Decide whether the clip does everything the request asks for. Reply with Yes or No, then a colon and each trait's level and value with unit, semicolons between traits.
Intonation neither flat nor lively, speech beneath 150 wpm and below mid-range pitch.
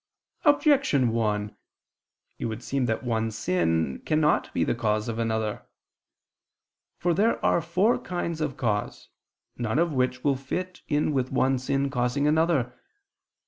No: wide, 5.8 semitones; average, 140 wpm; low, 130 Hz